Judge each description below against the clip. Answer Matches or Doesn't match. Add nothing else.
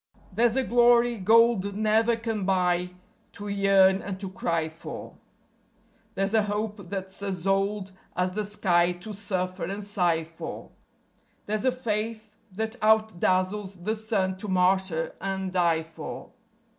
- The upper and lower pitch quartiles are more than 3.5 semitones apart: Doesn't match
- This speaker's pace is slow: Doesn't match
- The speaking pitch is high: Matches